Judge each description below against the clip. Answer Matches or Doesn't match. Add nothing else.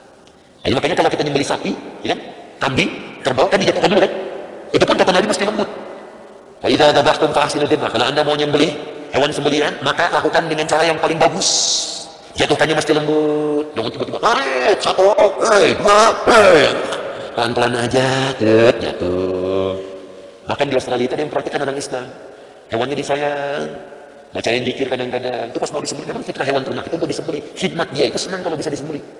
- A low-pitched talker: Doesn't match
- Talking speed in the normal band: Doesn't match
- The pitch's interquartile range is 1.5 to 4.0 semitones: Matches